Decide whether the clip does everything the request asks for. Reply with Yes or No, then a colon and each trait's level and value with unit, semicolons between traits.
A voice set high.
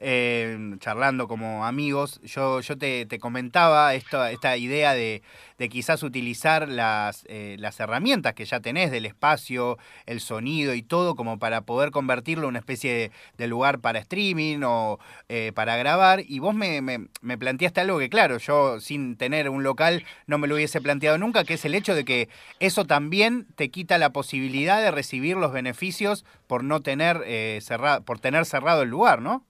No: low, 135 Hz